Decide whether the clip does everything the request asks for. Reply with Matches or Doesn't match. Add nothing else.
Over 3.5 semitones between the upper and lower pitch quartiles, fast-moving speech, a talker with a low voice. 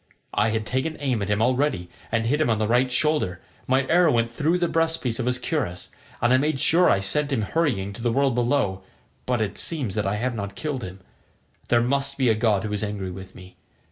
Matches